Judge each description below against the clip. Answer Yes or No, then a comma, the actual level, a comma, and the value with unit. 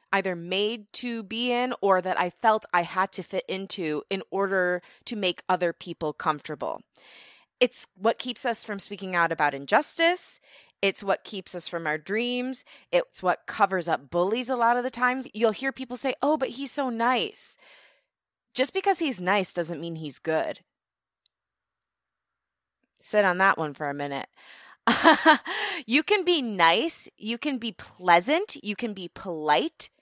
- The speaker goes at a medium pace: Yes, average, 165 wpm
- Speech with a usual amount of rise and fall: No, wide, 6.1 semitones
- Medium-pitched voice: No, high, 210 Hz